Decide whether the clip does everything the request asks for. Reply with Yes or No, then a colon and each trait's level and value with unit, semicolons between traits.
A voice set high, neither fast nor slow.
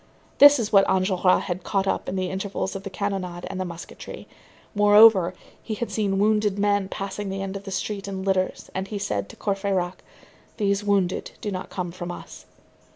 Yes: high, 195 Hz; average, 185 wpm